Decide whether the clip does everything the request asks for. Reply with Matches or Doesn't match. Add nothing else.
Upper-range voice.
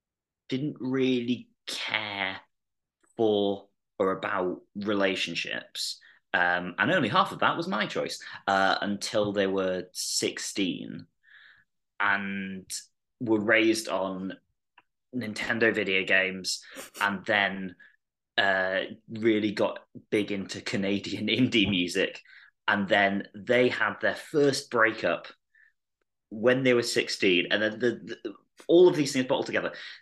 Doesn't match